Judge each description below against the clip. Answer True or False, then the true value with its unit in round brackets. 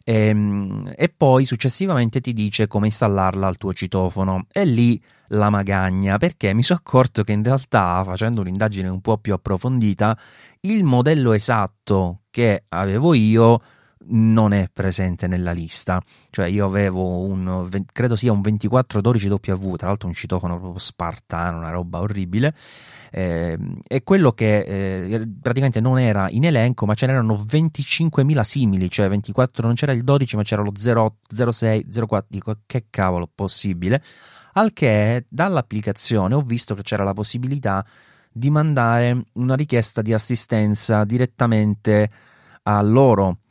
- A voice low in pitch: True (110 Hz)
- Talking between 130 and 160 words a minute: True (145 wpm)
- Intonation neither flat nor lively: True (4.2 semitones)